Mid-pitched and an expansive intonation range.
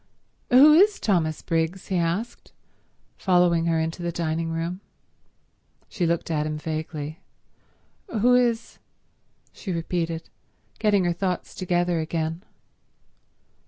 No: medium, 170 Hz; average, 2.8 semitones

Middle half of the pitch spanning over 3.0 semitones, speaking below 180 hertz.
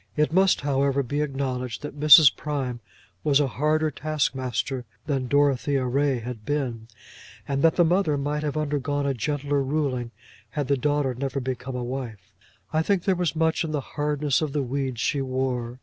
No: narrow, 2.6 semitones; medium, 140 Hz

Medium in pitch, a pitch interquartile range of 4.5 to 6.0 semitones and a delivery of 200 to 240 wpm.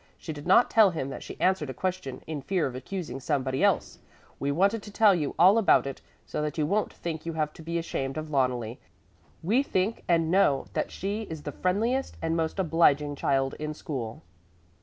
Yes: medium, 160 Hz; average, 5.0 semitones; fast, 205 wpm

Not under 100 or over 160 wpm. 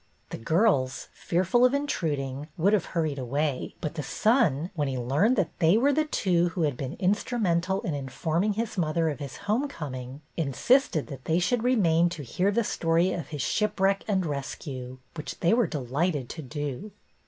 No: average, 185 wpm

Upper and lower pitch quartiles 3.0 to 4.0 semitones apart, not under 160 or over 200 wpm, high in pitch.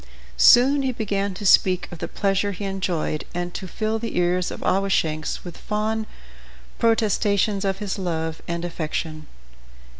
No: average, 3.3 semitones; average, 150 wpm; high, 195 Hz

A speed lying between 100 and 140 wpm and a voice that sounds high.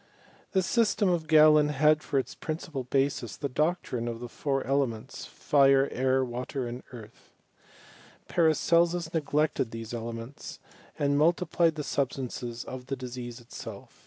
No: slow, 135 wpm; low, 135 Hz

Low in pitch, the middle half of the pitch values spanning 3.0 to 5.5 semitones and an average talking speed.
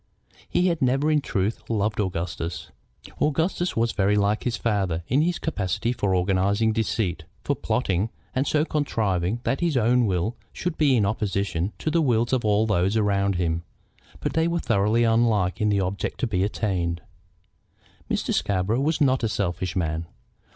Yes: low, 105 Hz; average, 4.9 semitones; average, 170 wpm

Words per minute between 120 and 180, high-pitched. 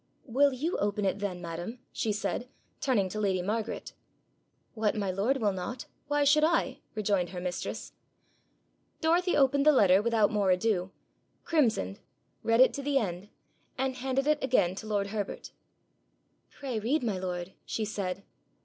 Yes: average, 160 wpm; high, 215 Hz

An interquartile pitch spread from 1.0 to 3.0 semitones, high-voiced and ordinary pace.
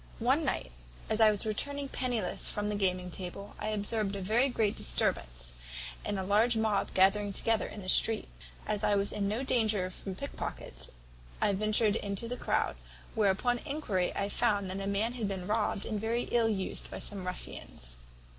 Yes: average, 2.7 semitones; high, 205 Hz; average, 185 wpm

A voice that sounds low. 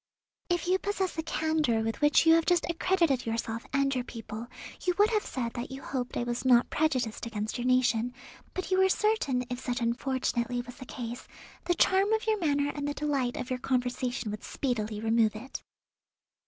No: very high, 255 Hz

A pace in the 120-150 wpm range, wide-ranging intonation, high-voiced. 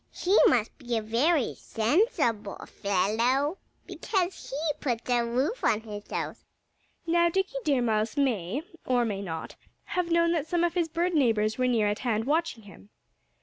No: average, 165 wpm; wide, 7.3 semitones; very high, 250 Hz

